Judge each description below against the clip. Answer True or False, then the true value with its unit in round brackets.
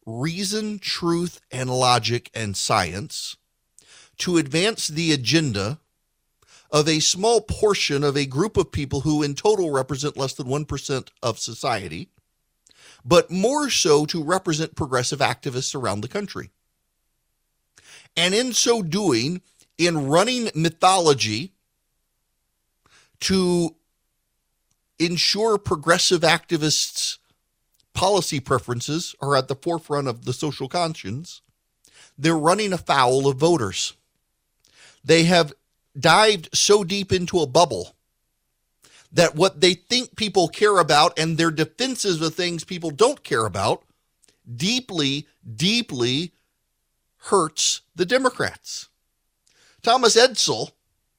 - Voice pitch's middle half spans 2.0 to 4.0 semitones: False (4.8 semitones)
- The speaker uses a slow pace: True (110 wpm)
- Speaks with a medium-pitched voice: True (165 Hz)